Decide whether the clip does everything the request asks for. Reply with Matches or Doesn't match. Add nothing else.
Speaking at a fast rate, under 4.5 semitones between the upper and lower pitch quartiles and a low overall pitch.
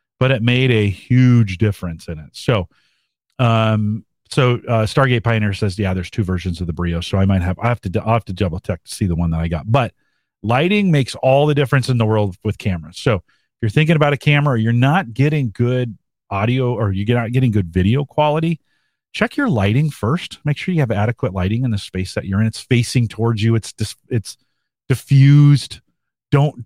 Doesn't match